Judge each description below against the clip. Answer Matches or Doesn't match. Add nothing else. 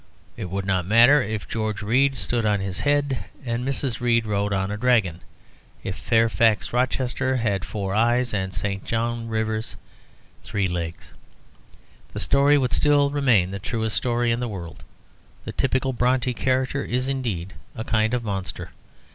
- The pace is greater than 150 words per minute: Matches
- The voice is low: Matches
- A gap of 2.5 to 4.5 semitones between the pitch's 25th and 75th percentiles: Matches